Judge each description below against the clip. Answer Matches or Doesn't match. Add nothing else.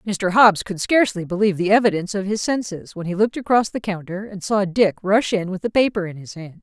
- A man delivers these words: Doesn't match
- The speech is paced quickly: Matches